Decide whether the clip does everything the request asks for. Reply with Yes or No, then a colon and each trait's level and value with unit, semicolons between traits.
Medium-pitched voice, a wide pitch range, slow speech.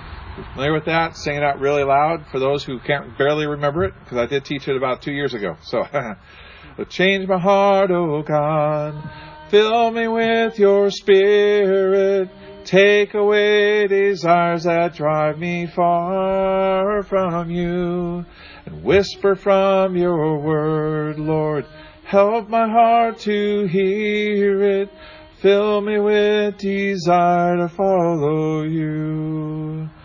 No: medium, 175 Hz; average, 4.6 semitones; slow, 125 wpm